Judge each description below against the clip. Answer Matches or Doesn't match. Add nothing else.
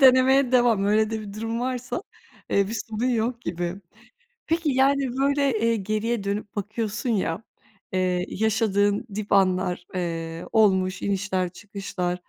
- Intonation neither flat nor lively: Matches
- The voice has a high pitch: Matches